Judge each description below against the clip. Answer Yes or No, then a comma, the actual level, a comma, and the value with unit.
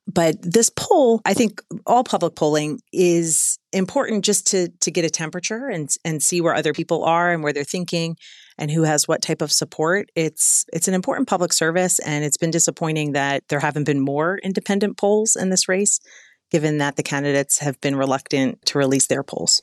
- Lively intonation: No, average, 4.0 semitones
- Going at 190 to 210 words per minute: Yes, average, 200 wpm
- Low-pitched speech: No, medium, 165 Hz